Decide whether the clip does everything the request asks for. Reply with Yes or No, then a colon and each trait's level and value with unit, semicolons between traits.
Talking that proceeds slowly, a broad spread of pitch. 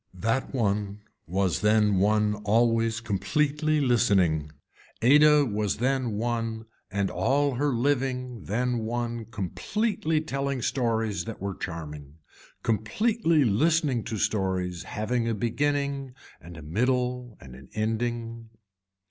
No: slow, 115 wpm; average, 4.5 semitones